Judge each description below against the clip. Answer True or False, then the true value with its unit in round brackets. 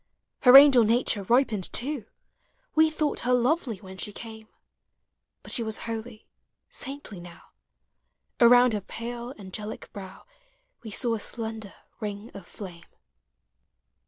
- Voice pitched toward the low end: False (225 Hz)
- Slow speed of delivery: True (130 wpm)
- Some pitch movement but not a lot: True (3.2 semitones)